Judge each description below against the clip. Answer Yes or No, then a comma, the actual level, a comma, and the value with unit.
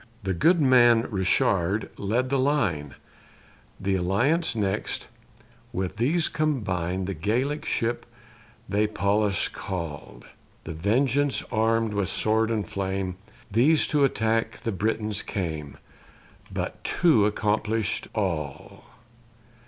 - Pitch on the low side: Yes, low, 105 Hz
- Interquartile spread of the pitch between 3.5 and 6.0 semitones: Yes, average, 4.1 semitones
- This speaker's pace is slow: Yes, slow, 110 wpm